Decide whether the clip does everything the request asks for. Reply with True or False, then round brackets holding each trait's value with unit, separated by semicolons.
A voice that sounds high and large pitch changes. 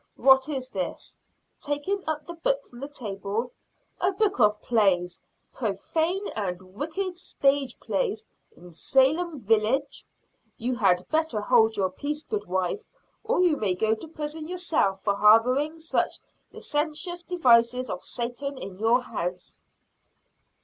True (265 Hz; 7.2 semitones)